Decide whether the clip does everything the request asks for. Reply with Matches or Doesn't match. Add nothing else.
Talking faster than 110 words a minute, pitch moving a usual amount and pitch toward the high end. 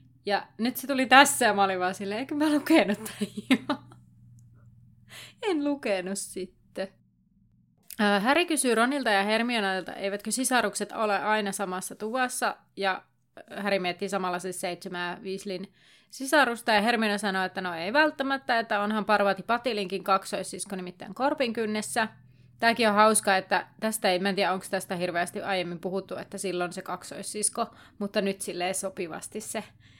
Matches